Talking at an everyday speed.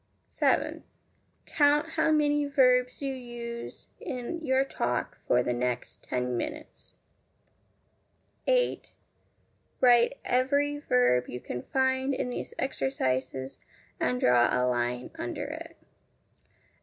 No: slow, 110 wpm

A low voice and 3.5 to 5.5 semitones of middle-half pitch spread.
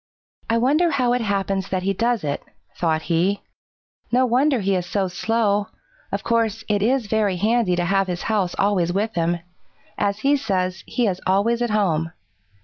No: high, 200 Hz; average, 4.1 semitones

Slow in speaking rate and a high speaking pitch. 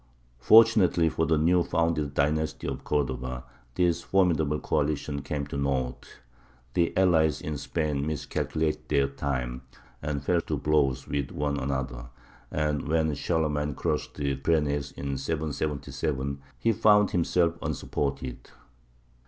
No: slow, 125 wpm; very low, 75 Hz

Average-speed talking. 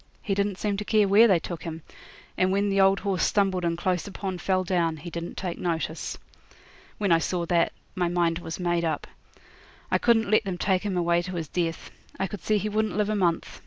No: fast, 225 wpm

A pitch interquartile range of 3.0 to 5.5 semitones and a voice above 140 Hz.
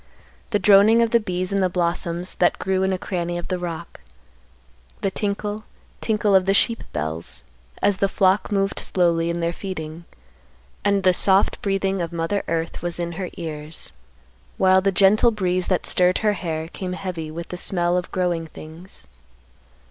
No: narrow, 2.5 semitones; medium, 185 Hz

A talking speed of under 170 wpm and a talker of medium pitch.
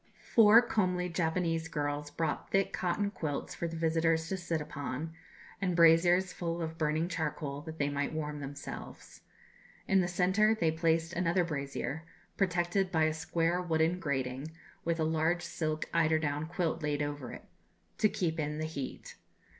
Yes: average, 160 wpm; medium, 165 Hz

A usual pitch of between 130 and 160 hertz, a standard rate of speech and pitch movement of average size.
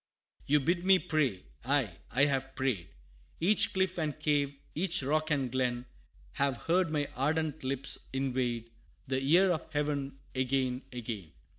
Yes: medium, 140 Hz; average, 150 wpm; average, 3.2 semitones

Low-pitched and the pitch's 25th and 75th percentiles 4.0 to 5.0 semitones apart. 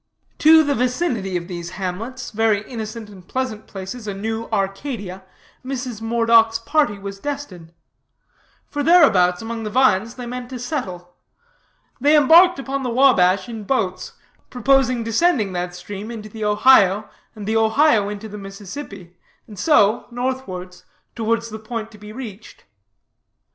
No: high, 225 Hz; average, 4.5 semitones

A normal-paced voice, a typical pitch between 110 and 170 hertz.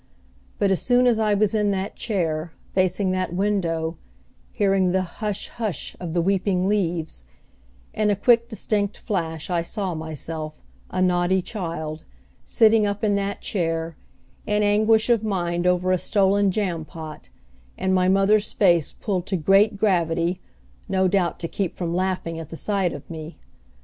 No: average, 160 wpm; medium, 185 Hz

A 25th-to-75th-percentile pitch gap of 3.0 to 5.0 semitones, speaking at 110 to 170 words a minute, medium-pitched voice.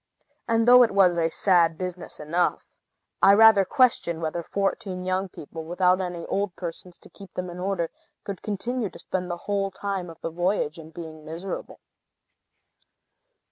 No: narrow, 2.6 semitones; average, 165 wpm; medium, 180 Hz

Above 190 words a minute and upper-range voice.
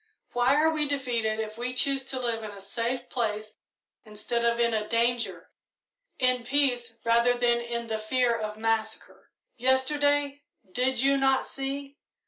No: average, 150 wpm; high, 240 Hz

